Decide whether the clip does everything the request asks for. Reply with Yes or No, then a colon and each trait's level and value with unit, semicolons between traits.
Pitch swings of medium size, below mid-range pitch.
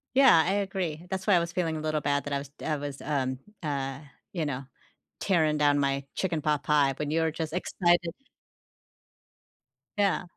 No: average, 3.3 semitones; medium, 155 Hz